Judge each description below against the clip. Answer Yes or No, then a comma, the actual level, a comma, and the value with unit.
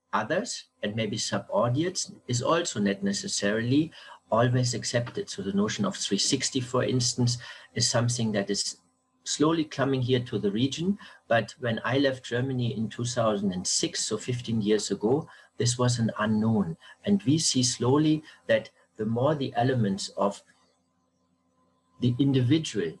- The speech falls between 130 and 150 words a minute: Yes, average, 140 wpm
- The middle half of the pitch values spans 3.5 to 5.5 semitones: Yes, average, 4.2 semitones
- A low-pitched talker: Yes, low, 120 Hz